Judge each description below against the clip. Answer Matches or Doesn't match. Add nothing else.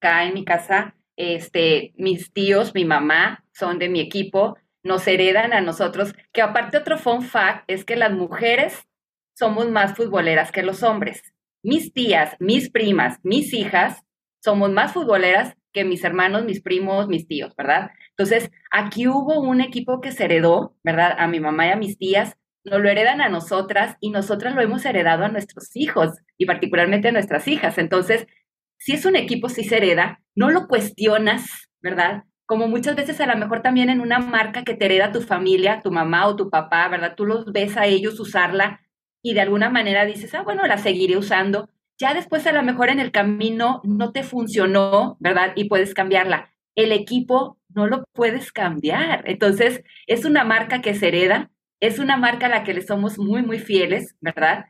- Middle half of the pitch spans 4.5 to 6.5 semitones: Doesn't match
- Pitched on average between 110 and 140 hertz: Doesn't match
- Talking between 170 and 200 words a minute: Matches